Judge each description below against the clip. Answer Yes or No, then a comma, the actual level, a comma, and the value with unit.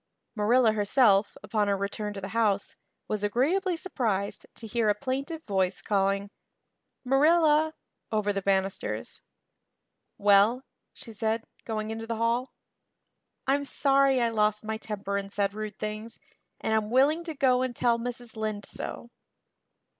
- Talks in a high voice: Yes, high, 220 Hz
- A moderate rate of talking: Yes, average, 145 wpm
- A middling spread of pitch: Yes, average, 3.7 semitones